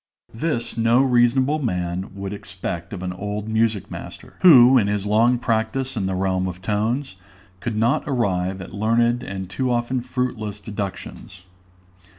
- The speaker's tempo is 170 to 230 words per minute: No, average, 155 wpm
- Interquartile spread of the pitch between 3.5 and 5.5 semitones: Yes, average, 4.0 semitones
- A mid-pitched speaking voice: No, low, 110 Hz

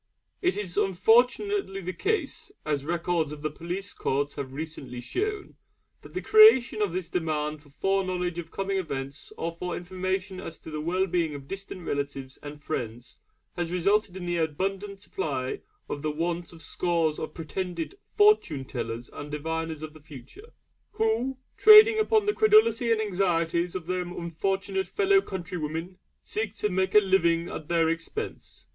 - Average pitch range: Yes, average, 4.1 semitones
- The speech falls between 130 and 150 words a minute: No, average, 165 wpm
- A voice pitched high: No, medium, 175 Hz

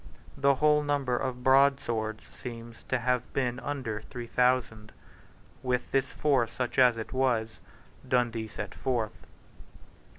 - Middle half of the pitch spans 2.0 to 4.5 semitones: Yes, narrow, 2.4 semitones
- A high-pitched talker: No, low, 125 Hz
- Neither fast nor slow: No, slow, 130 wpm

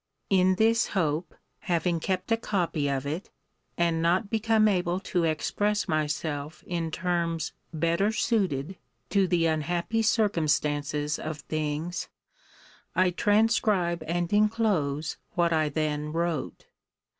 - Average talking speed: No, slow, 120 wpm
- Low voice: No, medium, 170 Hz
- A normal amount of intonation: Yes, average, 3.9 semitones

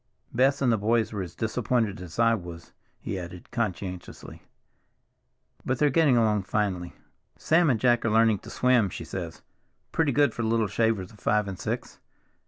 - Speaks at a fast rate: No, average, 170 wpm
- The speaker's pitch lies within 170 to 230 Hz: No, low, 110 Hz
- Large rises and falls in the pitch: No, average, 4.0 semitones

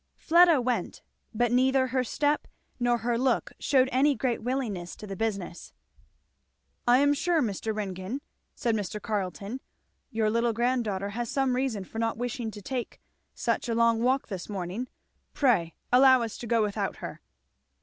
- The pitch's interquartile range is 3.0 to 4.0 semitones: Yes, average, 3.6 semitones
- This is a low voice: No, high, 235 Hz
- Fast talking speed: No, average, 160 wpm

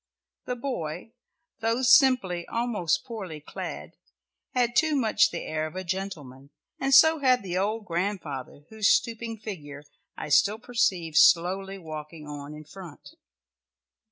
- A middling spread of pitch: No, wide, 6.8 semitones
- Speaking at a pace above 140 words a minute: No, slow, 135 wpm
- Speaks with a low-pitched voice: No, high, 190 Hz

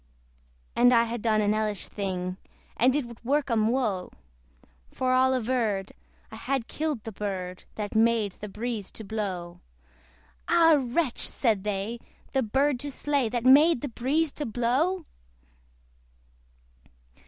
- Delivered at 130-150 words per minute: Yes, average, 140 wpm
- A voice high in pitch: Yes, high, 235 Hz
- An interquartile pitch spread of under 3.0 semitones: No, average, 4.0 semitones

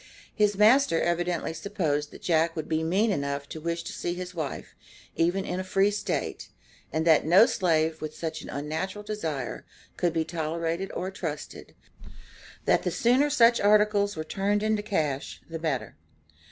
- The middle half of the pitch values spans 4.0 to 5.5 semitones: Yes, average, 4.3 semitones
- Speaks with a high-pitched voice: No, medium, 170 Hz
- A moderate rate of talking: Yes, average, 165 wpm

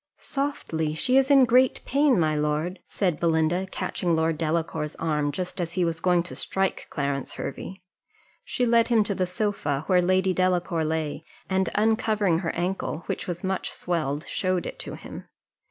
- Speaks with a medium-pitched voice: Yes, medium, 180 Hz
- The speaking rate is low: No, average, 170 wpm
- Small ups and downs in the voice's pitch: No, average, 3.4 semitones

